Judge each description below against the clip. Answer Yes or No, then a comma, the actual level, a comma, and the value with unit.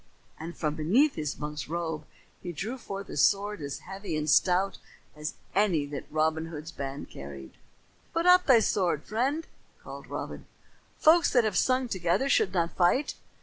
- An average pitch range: No, wide, 6.3 semitones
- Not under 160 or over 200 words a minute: Yes, average, 165 wpm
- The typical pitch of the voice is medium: Yes, medium, 175 Hz